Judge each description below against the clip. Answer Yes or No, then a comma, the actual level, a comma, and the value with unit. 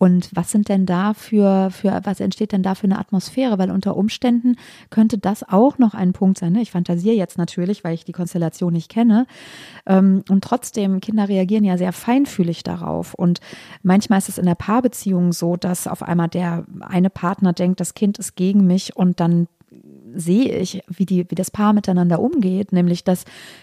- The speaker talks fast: Yes, fast, 195 wpm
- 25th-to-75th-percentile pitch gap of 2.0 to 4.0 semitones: Yes, average, 2.8 semitones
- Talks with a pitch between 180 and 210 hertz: Yes, high, 190 Hz